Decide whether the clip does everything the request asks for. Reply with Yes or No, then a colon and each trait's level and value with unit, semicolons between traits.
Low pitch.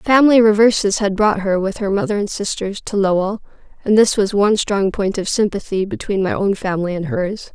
No: high, 205 Hz